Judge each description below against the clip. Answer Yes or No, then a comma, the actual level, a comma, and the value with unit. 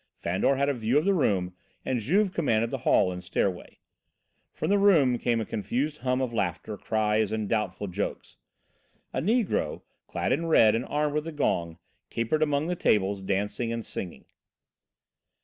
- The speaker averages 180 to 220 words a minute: No, average, 170 wpm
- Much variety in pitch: Yes, wide, 6.5 semitones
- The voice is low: Yes, low, 115 Hz